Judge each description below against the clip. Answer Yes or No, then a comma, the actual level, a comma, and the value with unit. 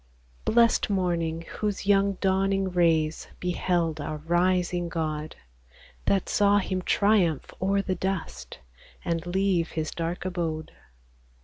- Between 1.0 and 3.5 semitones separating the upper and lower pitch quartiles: Yes, average, 2.9 semitones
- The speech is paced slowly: Yes, slow, 115 wpm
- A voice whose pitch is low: No, medium, 180 Hz